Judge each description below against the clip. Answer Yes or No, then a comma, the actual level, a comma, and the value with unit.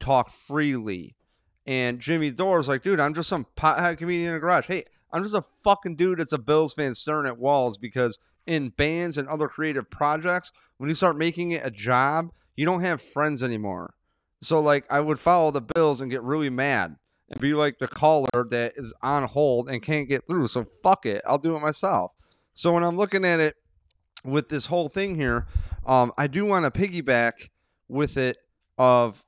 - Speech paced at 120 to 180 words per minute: No, average, 200 wpm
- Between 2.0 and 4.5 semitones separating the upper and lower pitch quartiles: No, average, 4.9 semitones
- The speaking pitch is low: No, medium, 145 Hz